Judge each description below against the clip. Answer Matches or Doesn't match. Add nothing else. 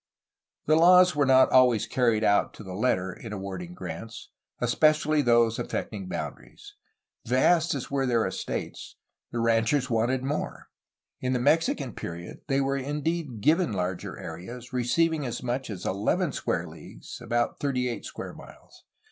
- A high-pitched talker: Doesn't match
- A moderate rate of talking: Matches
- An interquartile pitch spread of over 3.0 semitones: Matches